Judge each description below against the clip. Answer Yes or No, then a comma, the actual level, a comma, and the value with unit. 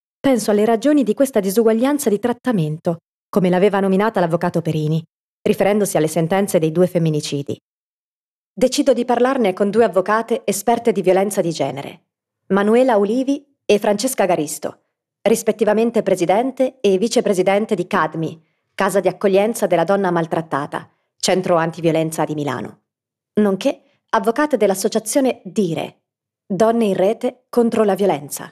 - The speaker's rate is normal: Yes, average, 130 wpm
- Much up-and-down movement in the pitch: No, average, 4.9 semitones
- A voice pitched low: No, high, 200 Hz